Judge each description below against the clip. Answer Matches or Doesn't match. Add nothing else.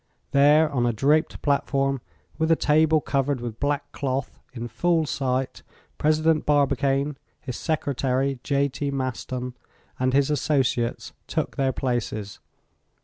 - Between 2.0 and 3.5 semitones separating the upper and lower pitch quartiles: Matches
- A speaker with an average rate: Doesn't match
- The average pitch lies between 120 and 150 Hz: Matches